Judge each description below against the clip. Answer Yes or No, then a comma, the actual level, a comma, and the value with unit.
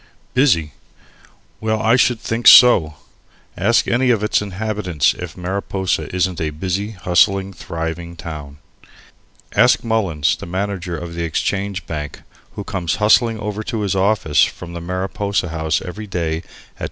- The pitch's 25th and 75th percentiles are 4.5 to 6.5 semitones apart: No, average, 4.0 semitones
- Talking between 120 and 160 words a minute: Yes, average, 150 wpm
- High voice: No, very low, 95 Hz